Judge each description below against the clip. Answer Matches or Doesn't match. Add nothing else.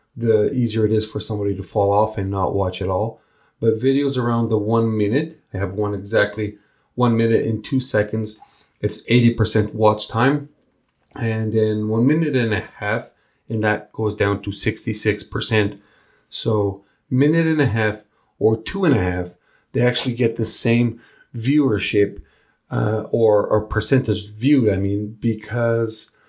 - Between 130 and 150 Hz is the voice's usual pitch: Doesn't match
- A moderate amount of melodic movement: Doesn't match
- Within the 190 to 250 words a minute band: Doesn't match